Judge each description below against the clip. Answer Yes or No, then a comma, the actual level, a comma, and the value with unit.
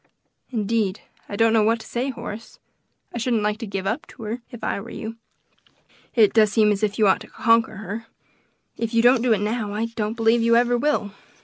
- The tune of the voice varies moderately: No, narrow, 1.8 semitones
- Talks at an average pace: No, fast, 230 wpm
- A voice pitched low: No, high, 225 Hz